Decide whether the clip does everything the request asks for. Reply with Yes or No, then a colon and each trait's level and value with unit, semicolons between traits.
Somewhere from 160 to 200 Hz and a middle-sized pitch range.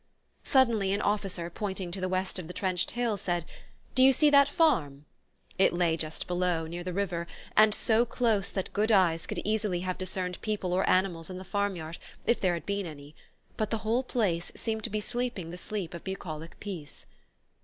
Yes: high, 190 Hz; average, 3.7 semitones